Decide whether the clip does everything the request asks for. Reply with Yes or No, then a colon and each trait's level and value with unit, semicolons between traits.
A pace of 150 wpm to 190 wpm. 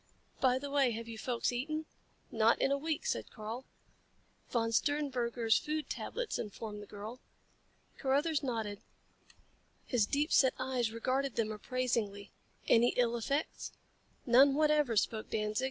No: average, 140 wpm